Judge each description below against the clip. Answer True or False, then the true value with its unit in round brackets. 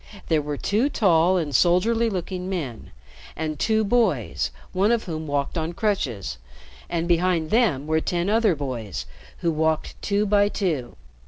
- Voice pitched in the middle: True (170 Hz)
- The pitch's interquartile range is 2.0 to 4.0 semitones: False (5.3 semitones)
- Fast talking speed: False (155 wpm)